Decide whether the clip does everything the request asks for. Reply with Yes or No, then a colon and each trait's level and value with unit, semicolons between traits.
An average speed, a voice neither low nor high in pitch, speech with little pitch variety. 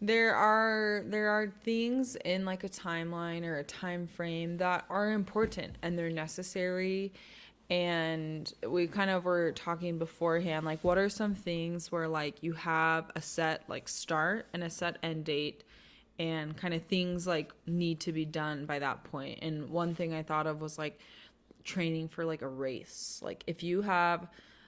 Yes: average, 180 wpm; medium, 170 Hz; narrow, 2.3 semitones